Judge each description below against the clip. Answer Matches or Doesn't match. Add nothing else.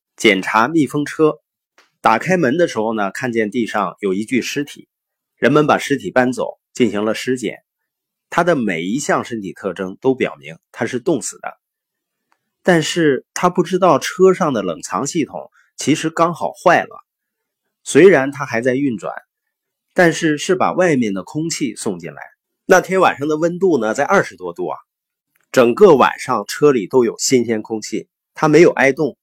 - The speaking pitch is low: Doesn't match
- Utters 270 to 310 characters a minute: Doesn't match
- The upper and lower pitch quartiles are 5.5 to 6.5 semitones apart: Matches